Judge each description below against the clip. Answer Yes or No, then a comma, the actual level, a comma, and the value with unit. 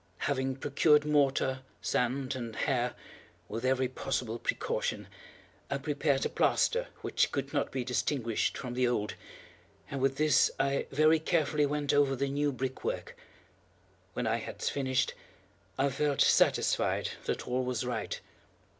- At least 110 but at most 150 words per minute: Yes, average, 140 wpm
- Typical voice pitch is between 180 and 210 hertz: No, low, 135 Hz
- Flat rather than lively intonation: Yes, narrow, 2.3 semitones